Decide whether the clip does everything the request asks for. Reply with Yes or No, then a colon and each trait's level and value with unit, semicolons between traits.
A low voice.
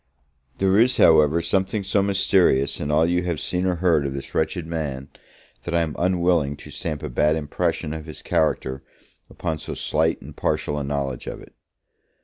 Yes: very low, 80 Hz